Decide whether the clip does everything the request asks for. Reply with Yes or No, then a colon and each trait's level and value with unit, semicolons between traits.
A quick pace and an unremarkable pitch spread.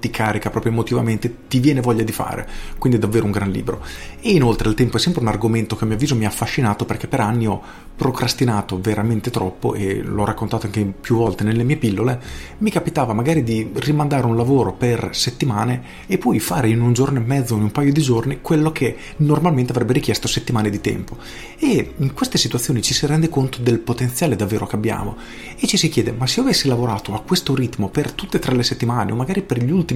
Yes: fast, 220 wpm; average, 3.7 semitones